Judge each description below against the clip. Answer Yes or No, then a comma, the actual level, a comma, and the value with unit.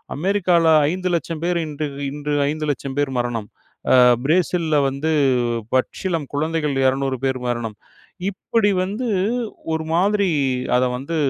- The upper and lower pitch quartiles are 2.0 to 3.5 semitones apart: No, average, 4.6 semitones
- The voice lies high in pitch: No, medium, 155 Hz